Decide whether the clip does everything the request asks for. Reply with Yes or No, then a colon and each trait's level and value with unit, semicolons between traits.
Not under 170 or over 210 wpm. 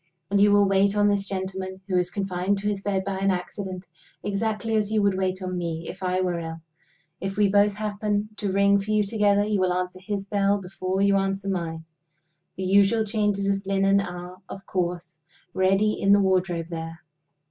Yes: average, 200 wpm